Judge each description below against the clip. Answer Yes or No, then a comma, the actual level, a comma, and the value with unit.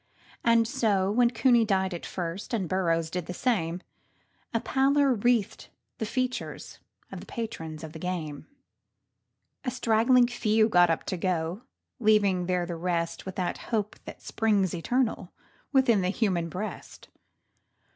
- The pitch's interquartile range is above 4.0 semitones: Yes, average, 4.8 semitones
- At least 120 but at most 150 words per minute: Yes, average, 145 wpm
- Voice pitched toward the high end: Yes, high, 200 Hz